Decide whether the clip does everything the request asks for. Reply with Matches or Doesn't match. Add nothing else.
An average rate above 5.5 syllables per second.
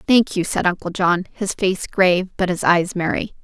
Doesn't match